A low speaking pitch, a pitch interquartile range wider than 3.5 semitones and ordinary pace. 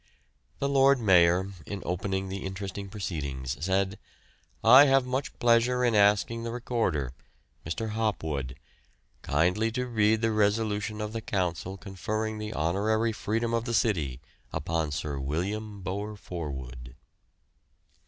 No: low, 100 Hz; average, 4.8 semitones; slow, 130 wpm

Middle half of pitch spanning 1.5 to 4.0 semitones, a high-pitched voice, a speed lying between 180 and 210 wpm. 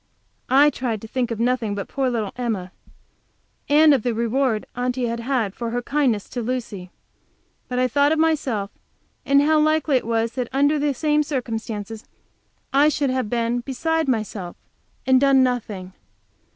No: average, 3.7 semitones; very high, 250 Hz; average, 165 wpm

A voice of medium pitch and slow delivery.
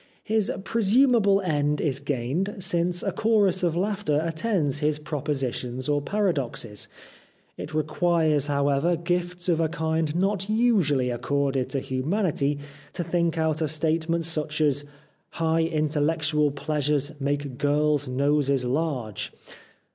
Yes: medium, 155 Hz; slow, 125 wpm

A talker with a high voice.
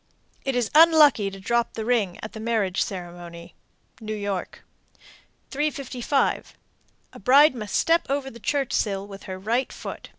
Yes: high, 225 Hz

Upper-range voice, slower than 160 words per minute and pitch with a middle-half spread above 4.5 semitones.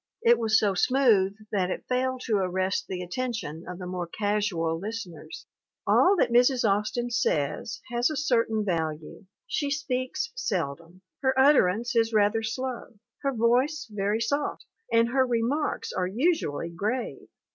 Yes: high, 225 Hz; average, 145 wpm; average, 5.3 semitones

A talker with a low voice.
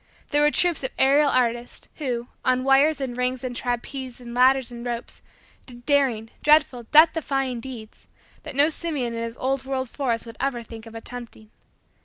No: very high, 255 Hz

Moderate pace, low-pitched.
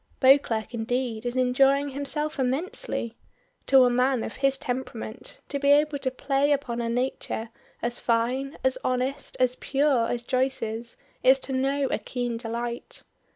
No: average, 155 wpm; very high, 255 Hz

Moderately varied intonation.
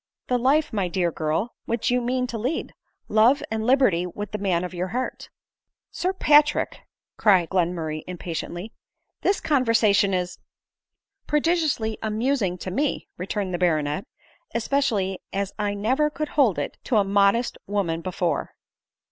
No: wide, 5.9 semitones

